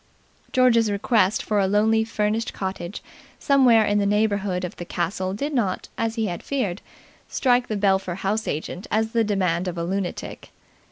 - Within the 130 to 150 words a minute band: No, average, 170 wpm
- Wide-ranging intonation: No, average, 3.0 semitones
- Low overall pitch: No, high, 205 Hz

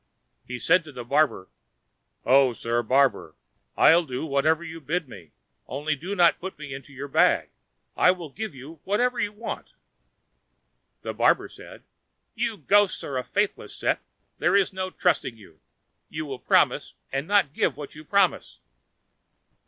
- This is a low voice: No, medium, 150 Hz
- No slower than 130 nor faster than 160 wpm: Yes, average, 155 wpm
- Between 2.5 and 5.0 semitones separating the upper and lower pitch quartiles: No, wide, 5.6 semitones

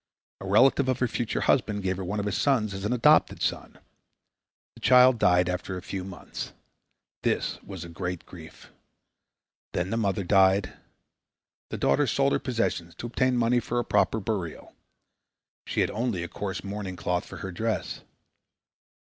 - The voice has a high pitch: No, low, 100 Hz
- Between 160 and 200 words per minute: Yes, average, 170 wpm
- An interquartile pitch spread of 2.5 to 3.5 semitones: No, average, 4.4 semitones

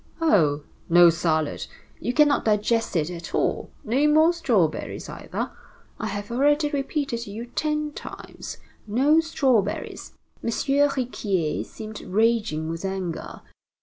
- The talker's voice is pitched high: Yes, high, 230 Hz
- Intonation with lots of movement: Yes, wide, 7.9 semitones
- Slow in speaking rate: Yes, slow, 125 wpm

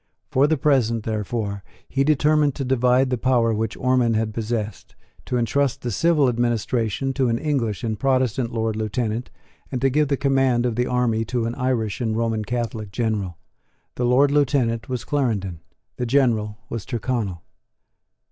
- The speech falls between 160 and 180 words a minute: Yes, average, 165 wpm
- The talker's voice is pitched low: Yes, low, 120 Hz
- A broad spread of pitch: No, average, 3.0 semitones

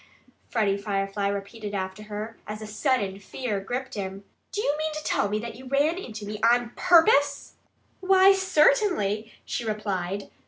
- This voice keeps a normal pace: Yes, average, 160 wpm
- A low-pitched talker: No, high, 220 Hz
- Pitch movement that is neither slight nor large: No, wide, 5.9 semitones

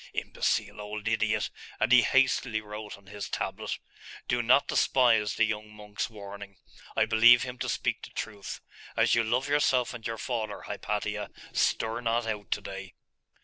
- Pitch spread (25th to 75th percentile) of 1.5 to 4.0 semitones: Yes, narrow, 2.4 semitones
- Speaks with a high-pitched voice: No, low, 110 Hz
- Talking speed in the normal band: Yes, average, 165 wpm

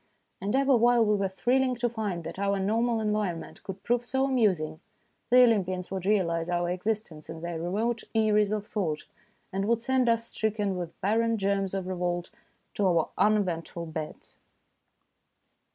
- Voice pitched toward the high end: Yes, high, 200 Hz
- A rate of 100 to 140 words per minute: No, average, 160 wpm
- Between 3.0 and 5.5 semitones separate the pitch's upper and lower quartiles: Yes, average, 4.3 semitones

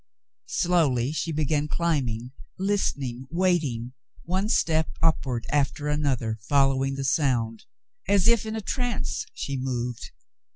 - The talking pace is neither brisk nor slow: No, slow, 120 wpm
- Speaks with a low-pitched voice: No, medium, 145 Hz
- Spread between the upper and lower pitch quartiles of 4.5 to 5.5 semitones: Yes, average, 5.1 semitones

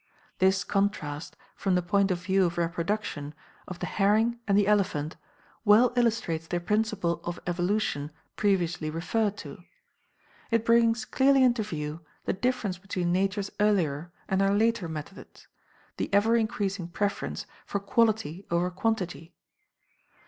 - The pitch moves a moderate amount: Yes, average, 3.8 semitones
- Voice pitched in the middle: No, high, 195 Hz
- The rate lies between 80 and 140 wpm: Yes, slow, 135 wpm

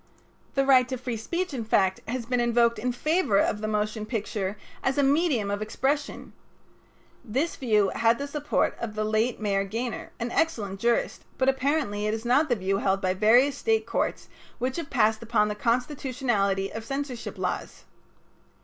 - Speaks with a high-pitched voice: Yes, high, 235 Hz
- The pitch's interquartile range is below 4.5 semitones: Yes, average, 4.1 semitones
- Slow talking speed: No, average, 175 wpm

